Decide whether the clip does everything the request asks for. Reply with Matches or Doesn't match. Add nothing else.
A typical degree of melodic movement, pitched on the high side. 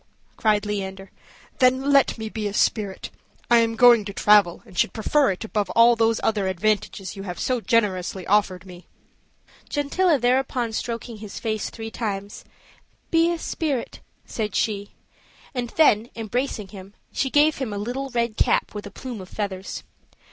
Matches